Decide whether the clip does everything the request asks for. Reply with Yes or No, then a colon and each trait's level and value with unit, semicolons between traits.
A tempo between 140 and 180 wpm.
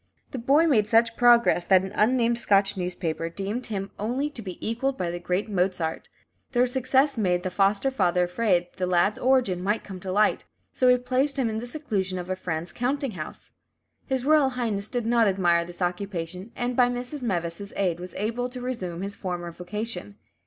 No: average, 195 wpm